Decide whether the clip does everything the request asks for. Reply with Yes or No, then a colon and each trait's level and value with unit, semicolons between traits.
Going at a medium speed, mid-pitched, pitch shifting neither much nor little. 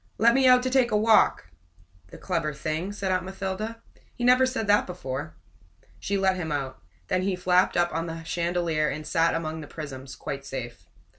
Yes: average, 195 wpm; medium, 180 Hz; average, 4.9 semitones